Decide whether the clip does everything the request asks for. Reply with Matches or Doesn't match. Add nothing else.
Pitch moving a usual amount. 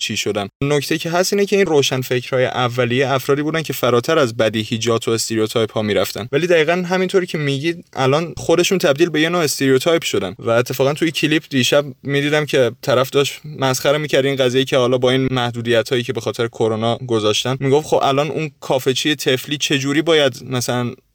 Matches